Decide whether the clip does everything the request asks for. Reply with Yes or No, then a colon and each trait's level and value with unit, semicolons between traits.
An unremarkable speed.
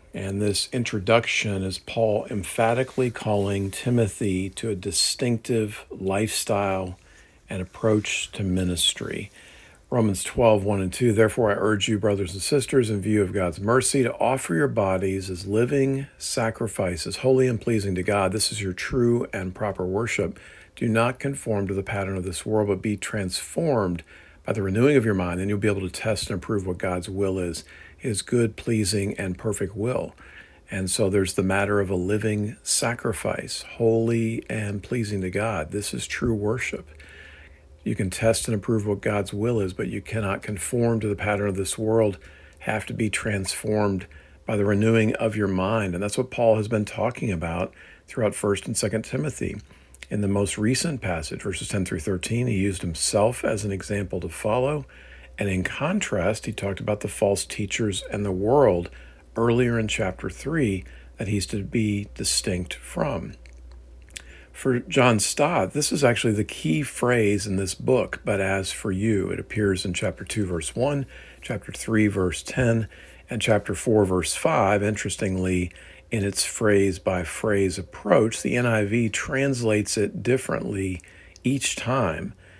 Yes: average, 170 wpm